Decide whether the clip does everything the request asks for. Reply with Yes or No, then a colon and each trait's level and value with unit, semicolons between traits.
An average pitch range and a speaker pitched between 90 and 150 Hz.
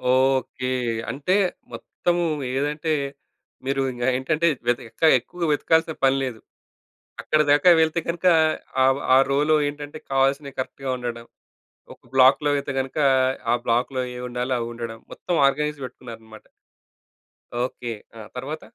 Yes: average, 3.1 semitones; low, 135 Hz